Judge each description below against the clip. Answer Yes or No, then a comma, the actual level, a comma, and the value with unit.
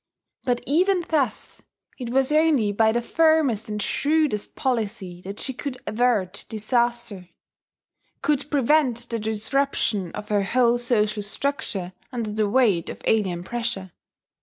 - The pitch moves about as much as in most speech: Yes, average, 4.4 semitones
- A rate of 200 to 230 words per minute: No, slow, 135 wpm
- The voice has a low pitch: No, high, 235 Hz